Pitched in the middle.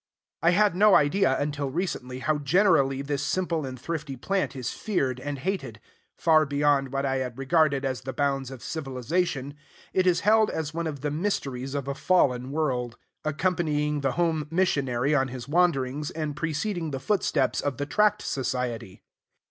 Yes: medium, 145 Hz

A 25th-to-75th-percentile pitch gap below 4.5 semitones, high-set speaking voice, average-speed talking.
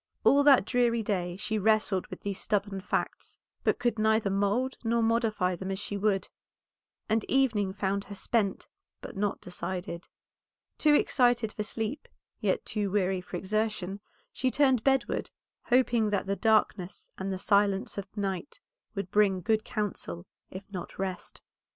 Yes: average, 2.8 semitones; high, 205 Hz; average, 155 wpm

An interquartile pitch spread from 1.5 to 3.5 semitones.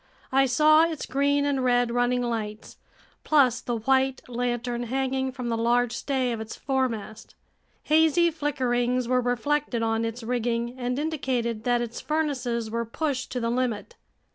Yes: narrow, 2.4 semitones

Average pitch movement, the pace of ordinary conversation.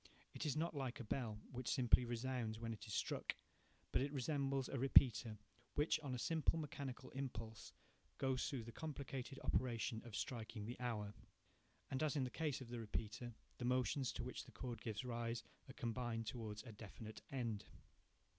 Yes: average, 3.0 semitones; average, 180 wpm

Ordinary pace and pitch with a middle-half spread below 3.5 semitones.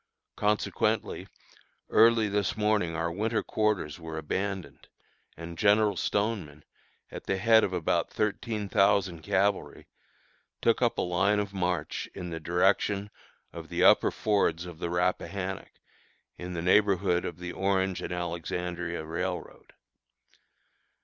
No: slow, 130 wpm; average, 2.9 semitones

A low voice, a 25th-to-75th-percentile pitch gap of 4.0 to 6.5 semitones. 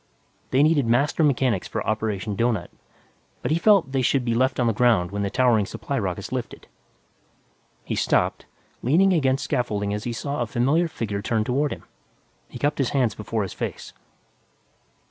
Yes: low, 120 Hz; average, 4.6 semitones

